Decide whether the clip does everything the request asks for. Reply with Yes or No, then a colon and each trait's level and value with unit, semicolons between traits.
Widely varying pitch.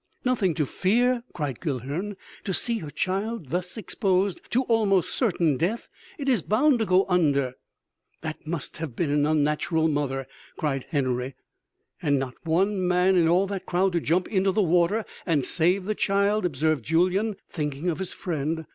No: average, 4.7 semitones